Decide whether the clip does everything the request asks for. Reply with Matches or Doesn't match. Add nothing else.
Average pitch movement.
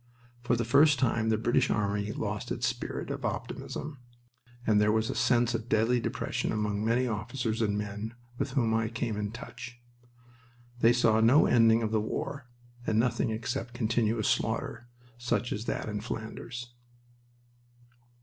Doesn't match